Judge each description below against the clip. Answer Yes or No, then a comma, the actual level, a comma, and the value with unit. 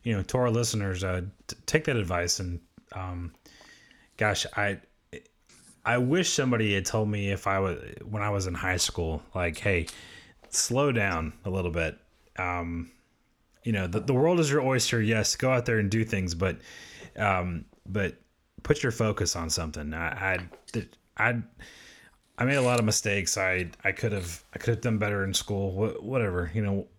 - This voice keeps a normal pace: Yes, average, 185 wpm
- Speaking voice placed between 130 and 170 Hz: No, low, 100 Hz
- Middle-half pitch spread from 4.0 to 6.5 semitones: Yes, average, 4.3 semitones